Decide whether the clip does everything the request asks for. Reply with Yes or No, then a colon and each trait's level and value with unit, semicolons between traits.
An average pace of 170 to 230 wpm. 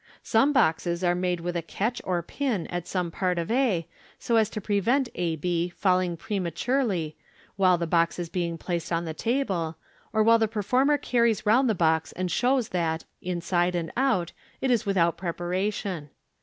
Yes: average, 180 wpm